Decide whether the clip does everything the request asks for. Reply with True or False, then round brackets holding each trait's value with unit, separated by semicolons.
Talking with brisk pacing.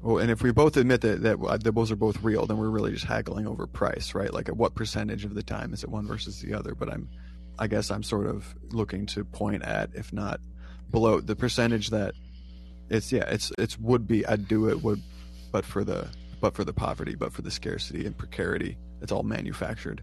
True (230 wpm)